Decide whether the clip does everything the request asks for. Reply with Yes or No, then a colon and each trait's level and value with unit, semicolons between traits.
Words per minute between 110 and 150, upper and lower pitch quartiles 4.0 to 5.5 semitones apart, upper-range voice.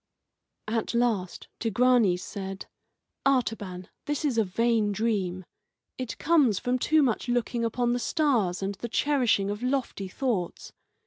Yes: slow, 135 wpm; average, 4.3 semitones; high, 230 Hz